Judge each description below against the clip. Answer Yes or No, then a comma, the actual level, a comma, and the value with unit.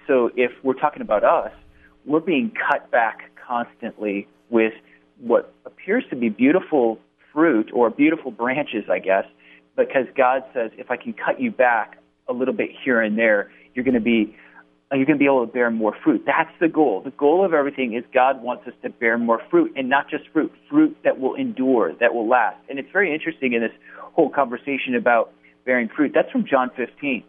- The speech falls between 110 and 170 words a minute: No, average, 200 wpm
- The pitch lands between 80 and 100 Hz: No, low, 125 Hz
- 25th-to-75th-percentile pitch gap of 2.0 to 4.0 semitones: No, average, 4.8 semitones